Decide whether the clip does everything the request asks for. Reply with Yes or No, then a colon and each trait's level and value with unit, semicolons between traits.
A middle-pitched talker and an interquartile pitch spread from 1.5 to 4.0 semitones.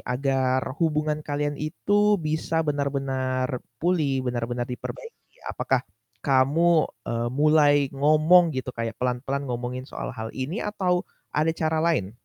Yes: medium, 145 Hz; average, 3.7 semitones